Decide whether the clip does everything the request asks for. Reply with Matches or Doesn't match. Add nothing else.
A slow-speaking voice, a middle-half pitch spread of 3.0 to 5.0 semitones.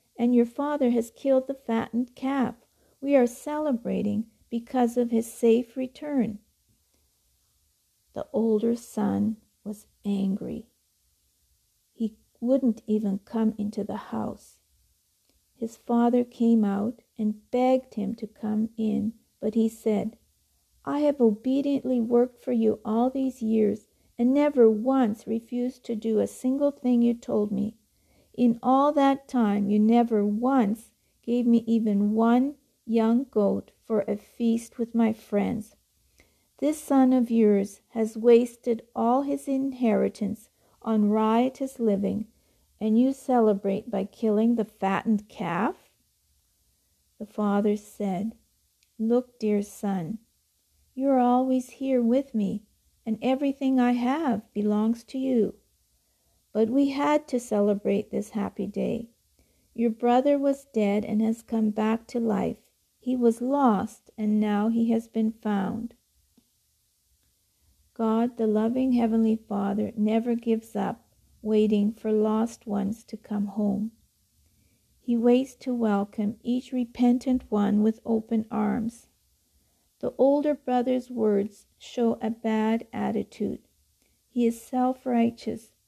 Doesn't match